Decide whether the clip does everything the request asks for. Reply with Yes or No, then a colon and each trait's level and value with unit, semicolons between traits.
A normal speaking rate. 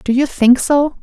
No: fast, 235 wpm